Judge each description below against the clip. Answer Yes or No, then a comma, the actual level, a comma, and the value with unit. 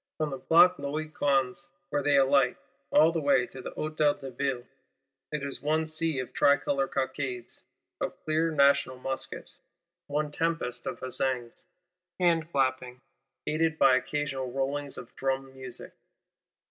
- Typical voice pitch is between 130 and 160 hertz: Yes, medium, 140 Hz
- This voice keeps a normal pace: Yes, average, 145 wpm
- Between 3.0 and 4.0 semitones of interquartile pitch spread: No, narrow, 2.6 semitones